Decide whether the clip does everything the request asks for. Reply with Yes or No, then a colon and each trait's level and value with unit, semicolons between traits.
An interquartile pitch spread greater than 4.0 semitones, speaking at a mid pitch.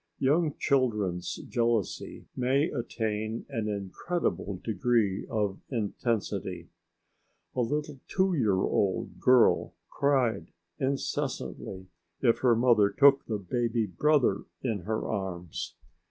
No: average, 4.6 semitones; low, 115 Hz